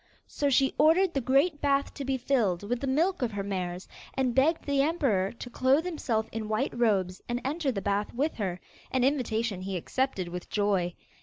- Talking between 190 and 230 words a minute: Yes, average, 200 wpm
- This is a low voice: No, high, 245 Hz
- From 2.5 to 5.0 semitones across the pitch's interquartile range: No, wide, 5.6 semitones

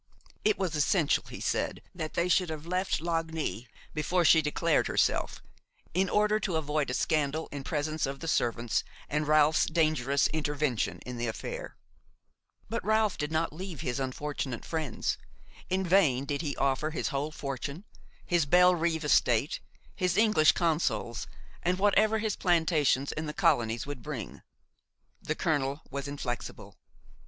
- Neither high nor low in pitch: Yes, medium, 155 Hz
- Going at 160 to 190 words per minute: No, average, 150 wpm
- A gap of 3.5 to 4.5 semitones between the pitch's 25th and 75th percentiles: Yes, average, 3.8 semitones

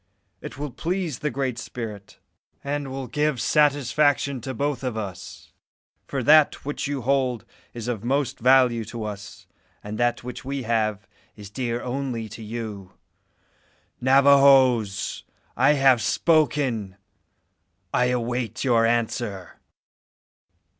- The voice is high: No, low, 125 Hz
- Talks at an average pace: No, slow, 125 wpm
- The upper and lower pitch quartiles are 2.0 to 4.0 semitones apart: Yes, average, 3.4 semitones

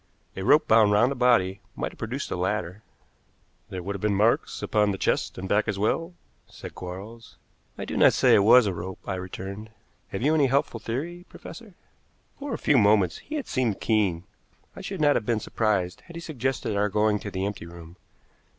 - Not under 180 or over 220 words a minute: Yes, fast, 205 wpm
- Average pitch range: Yes, average, 5.0 semitones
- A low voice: Yes, low, 105 Hz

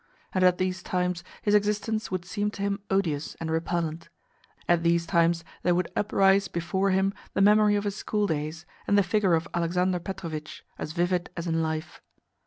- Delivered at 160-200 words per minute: Yes, average, 185 wpm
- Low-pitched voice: No, medium, 180 Hz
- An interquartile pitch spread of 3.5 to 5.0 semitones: No, average, 2.9 semitones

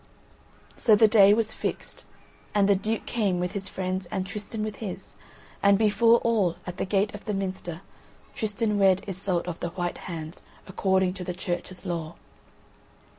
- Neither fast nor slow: Yes, average, 170 wpm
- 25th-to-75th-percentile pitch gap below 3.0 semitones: Yes, narrow, 2.6 semitones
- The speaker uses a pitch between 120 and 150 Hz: No, high, 195 Hz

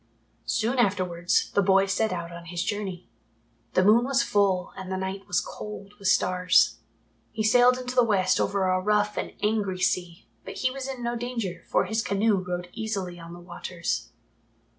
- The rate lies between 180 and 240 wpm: Yes, average, 185 wpm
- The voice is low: No, high, 195 Hz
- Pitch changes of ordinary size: Yes, average, 3.3 semitones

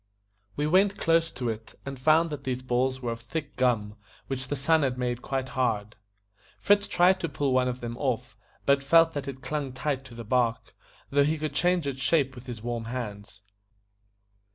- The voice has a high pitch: No, low, 130 Hz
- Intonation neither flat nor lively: Yes, average, 3.5 semitones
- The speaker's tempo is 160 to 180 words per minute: No, average, 200 wpm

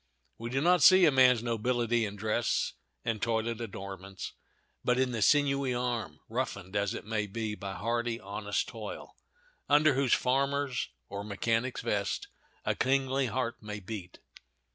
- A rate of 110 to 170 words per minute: Yes, average, 145 wpm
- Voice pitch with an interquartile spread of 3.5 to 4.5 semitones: Yes, average, 3.8 semitones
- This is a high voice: No, low, 115 Hz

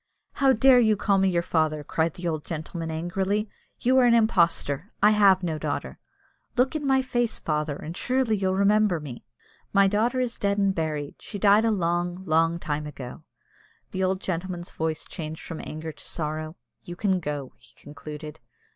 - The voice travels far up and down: No, average, 5.0 semitones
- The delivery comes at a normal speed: Yes, average, 180 wpm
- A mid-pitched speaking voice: Yes, medium, 180 Hz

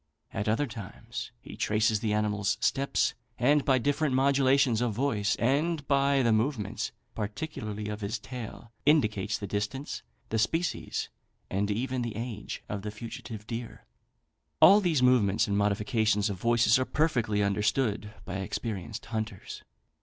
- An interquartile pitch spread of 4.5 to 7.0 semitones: No, average, 4.1 semitones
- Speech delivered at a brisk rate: No, average, 145 wpm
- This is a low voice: Yes, low, 115 Hz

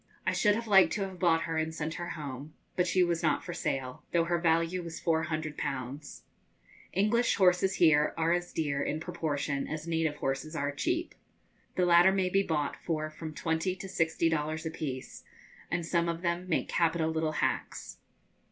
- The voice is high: No, medium, 165 Hz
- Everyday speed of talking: Yes, average, 180 wpm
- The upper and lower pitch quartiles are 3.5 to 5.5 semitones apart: No, narrow, 2.4 semitones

